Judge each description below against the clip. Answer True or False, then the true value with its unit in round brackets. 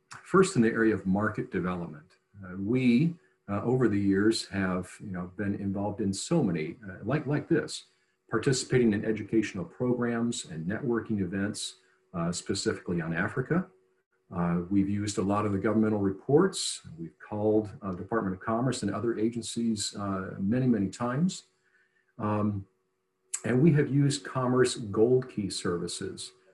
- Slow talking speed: False (150 wpm)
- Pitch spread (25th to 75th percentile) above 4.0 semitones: False (3.7 semitones)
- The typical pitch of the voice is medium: False (105 Hz)